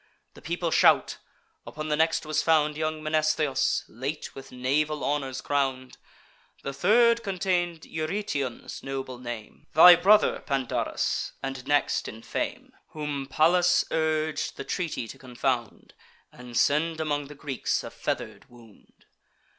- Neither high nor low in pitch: Yes, medium, 150 Hz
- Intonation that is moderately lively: Yes, average, 3.2 semitones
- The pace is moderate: No, slow, 130 wpm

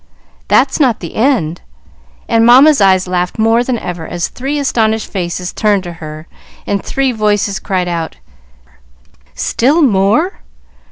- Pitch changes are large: Yes, wide, 5.7 semitones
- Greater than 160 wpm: No, slow, 135 wpm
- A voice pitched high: Yes, high, 210 Hz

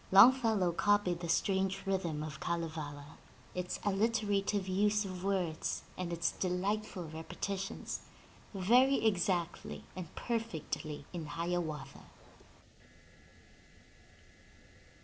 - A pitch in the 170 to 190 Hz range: Yes, medium, 185 Hz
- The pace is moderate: No, slow, 90 wpm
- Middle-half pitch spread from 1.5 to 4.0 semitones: Yes, average, 3.4 semitones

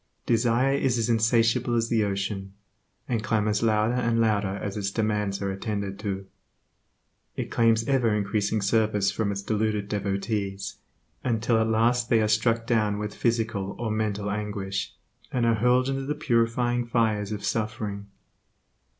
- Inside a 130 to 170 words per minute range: Yes, average, 150 wpm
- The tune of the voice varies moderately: No, narrow, 2.3 semitones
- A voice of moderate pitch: No, low, 110 Hz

